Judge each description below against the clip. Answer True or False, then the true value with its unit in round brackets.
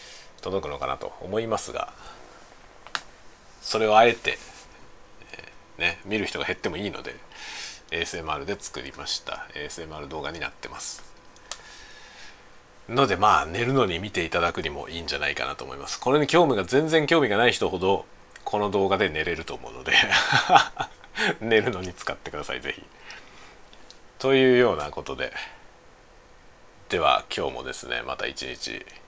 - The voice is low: True (110 Hz)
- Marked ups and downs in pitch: True (6.5 semitones)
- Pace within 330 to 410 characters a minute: False (305 characters per minute)